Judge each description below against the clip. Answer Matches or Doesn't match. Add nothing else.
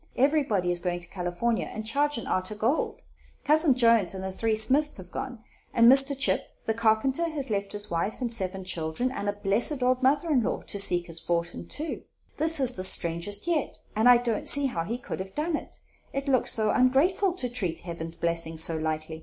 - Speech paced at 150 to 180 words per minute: Doesn't match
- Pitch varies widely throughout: Matches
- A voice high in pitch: Matches